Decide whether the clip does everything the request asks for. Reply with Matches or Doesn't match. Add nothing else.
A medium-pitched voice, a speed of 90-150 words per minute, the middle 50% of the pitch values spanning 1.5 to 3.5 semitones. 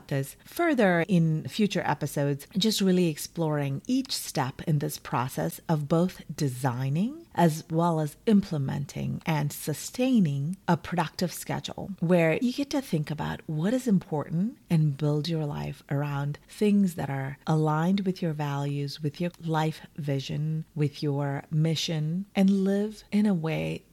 Doesn't match